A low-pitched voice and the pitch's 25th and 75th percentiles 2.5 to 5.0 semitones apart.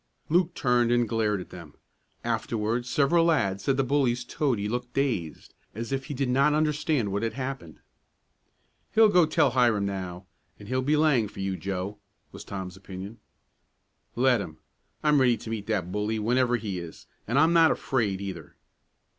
No: low, 120 Hz; wide, 5.4 semitones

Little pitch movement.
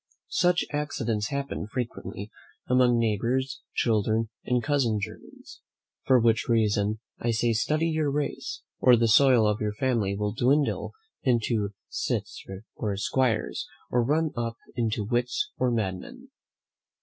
No: average, 3.5 semitones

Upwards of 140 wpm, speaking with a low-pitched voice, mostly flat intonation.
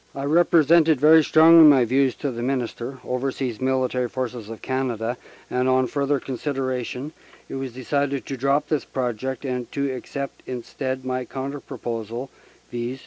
Yes: average, 155 wpm; low, 130 Hz; narrow, 2.0 semitones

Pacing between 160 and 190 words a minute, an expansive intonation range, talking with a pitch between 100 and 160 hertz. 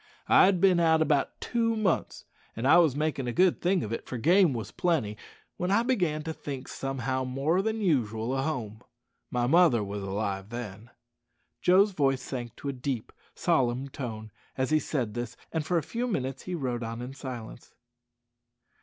Yes: average, 180 wpm; wide, 6.2 semitones; low, 135 Hz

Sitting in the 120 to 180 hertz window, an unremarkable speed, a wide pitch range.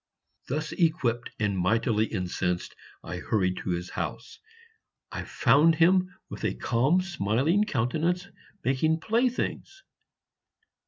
No: low, 135 Hz; slow, 110 wpm; wide, 8.9 semitones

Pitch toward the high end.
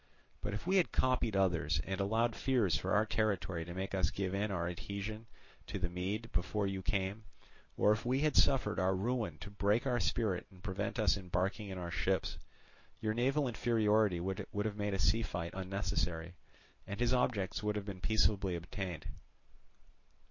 No: low, 100 Hz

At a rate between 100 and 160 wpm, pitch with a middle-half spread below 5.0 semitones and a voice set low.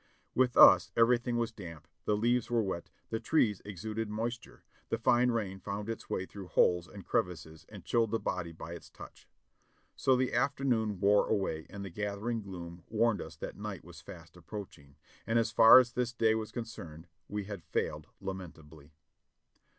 No: average, 180 wpm; average, 4.2 semitones; low, 105 Hz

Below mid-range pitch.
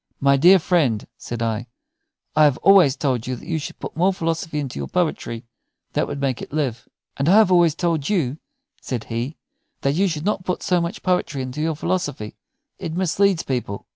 No: medium, 150 Hz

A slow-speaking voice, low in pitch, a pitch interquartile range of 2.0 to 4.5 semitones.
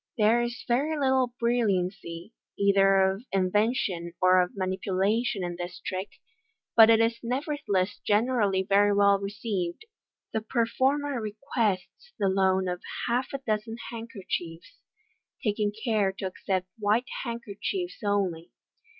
No: slow, 125 wpm; high, 205 Hz; average, 3.9 semitones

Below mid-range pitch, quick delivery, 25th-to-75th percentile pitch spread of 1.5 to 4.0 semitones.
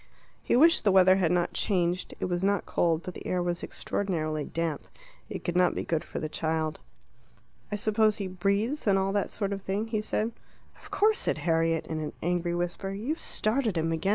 No: medium, 185 Hz; fast, 210 wpm; average, 3.5 semitones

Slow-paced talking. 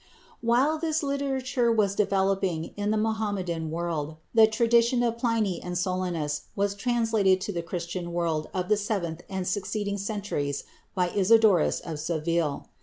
No: average, 145 wpm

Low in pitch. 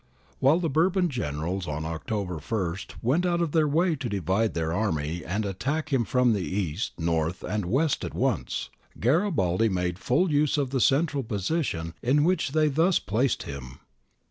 Yes: low, 115 Hz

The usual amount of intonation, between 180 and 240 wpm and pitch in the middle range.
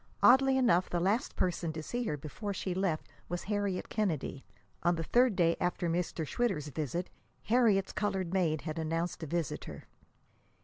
No: average, 4.0 semitones; average, 165 wpm; medium, 180 Hz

